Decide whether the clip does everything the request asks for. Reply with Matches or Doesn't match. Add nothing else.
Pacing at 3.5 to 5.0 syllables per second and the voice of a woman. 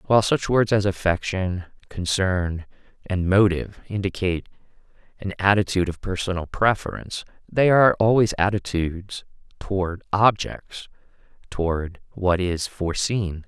Doesn't match